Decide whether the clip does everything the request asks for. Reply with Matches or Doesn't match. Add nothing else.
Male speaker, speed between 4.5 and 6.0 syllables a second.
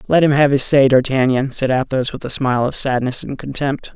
Matches